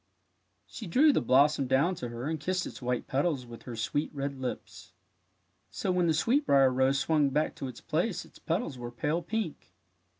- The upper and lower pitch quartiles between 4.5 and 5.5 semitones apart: Yes, average, 4.8 semitones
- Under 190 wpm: No, average, 195 wpm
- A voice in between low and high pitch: Yes, medium, 145 Hz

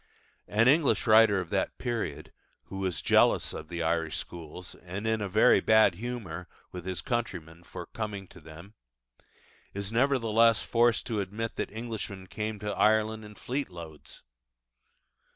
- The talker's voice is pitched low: Yes, low, 105 Hz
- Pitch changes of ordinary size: Yes, average, 4.1 semitones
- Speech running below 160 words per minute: Yes, average, 145 wpm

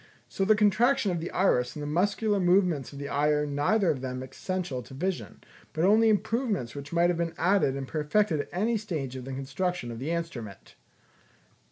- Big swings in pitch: Yes, wide, 6.1 semitones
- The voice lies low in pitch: No, medium, 170 Hz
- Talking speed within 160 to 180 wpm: No, average, 200 wpm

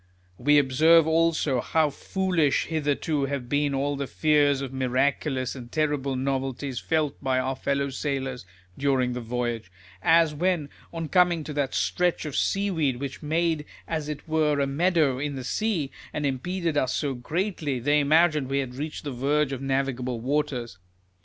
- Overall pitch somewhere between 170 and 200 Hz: No, medium, 145 Hz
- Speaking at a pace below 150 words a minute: No, average, 165 wpm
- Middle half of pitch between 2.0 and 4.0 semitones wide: Yes, average, 3.0 semitones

